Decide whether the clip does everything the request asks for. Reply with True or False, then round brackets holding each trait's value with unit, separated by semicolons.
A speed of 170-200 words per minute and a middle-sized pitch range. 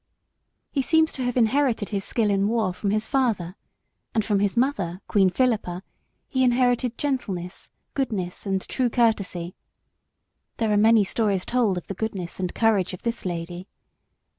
False (160 wpm; 4.6 semitones)